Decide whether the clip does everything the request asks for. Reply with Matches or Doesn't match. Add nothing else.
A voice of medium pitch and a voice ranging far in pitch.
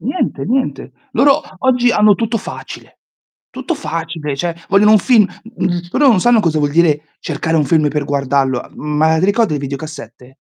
Matches